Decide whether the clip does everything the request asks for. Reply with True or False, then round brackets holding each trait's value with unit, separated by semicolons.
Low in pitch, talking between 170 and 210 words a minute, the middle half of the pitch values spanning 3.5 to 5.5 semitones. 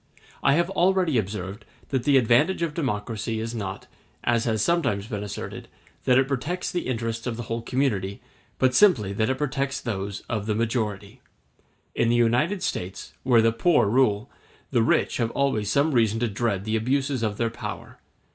True (115 Hz; 180 wpm; 4.2 semitones)